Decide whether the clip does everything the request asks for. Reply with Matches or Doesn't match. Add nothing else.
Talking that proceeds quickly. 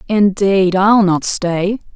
Doesn't match